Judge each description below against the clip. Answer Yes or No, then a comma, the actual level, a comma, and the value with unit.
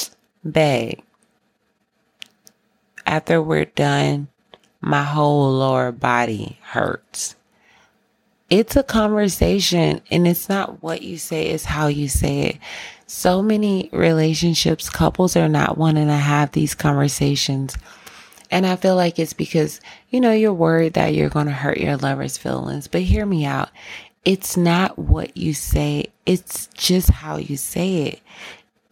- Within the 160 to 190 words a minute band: No, average, 140 wpm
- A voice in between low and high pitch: Yes, medium, 155 Hz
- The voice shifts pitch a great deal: No, average, 4.6 semitones